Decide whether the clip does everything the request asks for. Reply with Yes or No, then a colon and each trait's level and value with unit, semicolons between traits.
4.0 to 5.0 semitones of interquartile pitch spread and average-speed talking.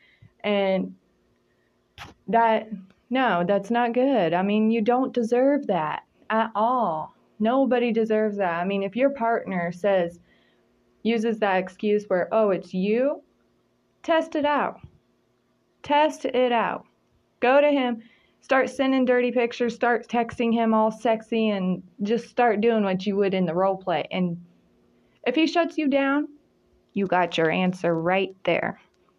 Yes: average, 4.7 semitones; average, 145 wpm